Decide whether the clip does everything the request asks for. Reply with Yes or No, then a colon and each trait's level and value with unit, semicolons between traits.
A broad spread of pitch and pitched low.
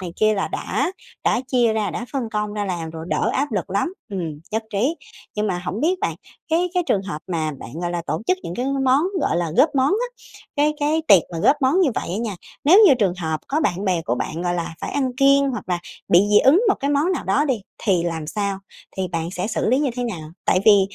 No: wide, 7.8 semitones; high, 210 Hz